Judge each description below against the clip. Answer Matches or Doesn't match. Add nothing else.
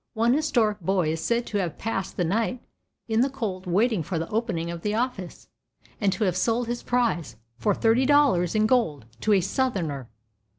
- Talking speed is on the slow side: Doesn't match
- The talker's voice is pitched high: Matches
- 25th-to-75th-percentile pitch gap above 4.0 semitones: Matches